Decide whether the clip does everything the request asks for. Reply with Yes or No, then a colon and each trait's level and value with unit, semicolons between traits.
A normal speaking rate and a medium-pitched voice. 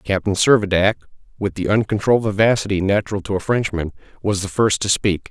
No: average, 170 wpm; low, 100 Hz